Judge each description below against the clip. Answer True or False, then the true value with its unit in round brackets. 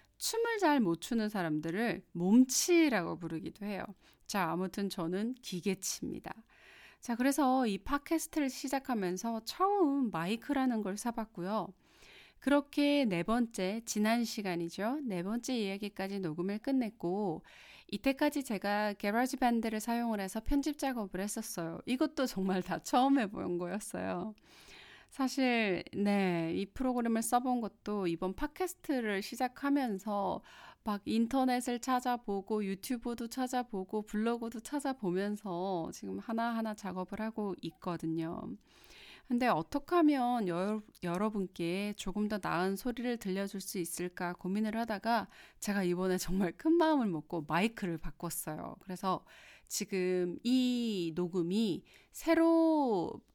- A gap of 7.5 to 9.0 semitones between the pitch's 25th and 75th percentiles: False (5.2 semitones)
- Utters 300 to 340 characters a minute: False (285 characters per minute)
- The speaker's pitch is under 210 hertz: False (215 Hz)